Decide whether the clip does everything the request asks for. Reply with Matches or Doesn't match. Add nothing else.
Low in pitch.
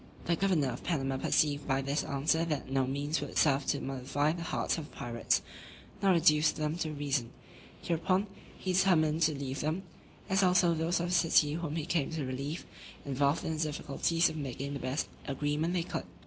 Doesn't match